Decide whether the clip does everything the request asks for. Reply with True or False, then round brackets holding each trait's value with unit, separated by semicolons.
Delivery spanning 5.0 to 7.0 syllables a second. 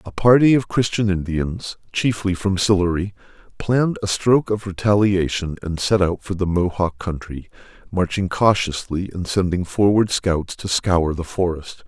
False (4.6 syllables/s)